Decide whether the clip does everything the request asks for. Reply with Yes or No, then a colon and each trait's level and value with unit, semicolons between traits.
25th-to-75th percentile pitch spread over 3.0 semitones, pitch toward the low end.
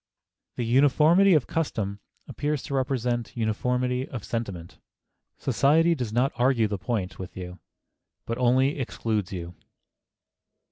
Yes: average, 4.1 semitones; low, 125 Hz